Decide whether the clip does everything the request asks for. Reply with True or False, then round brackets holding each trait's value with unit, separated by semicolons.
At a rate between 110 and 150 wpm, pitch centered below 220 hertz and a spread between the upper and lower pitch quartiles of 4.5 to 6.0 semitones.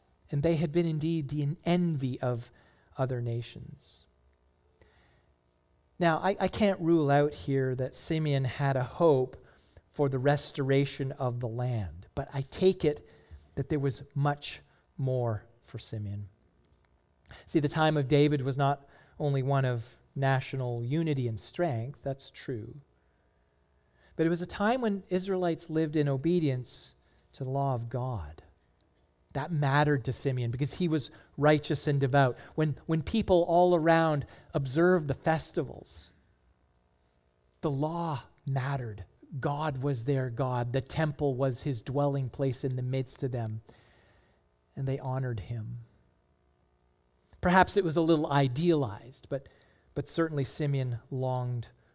True (140 wpm; 135 Hz; 5.3 semitones)